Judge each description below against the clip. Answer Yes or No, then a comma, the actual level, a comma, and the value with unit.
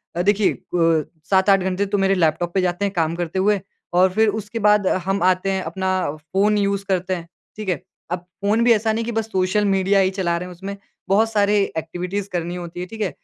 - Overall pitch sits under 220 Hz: Yes, high, 190 Hz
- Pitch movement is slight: Yes, narrow, 2.3 semitones